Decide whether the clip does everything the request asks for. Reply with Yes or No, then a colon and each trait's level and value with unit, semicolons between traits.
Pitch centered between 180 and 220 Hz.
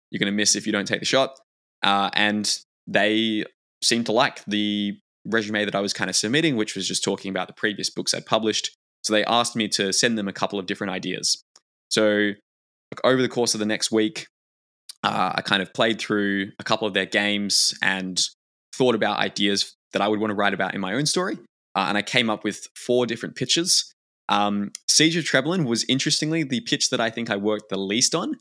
No: low, 105 Hz